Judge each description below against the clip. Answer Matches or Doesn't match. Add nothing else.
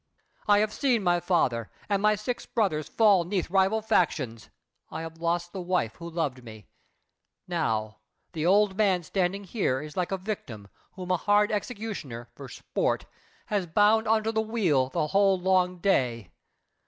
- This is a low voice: Doesn't match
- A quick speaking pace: Doesn't match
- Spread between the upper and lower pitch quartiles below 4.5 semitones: Doesn't match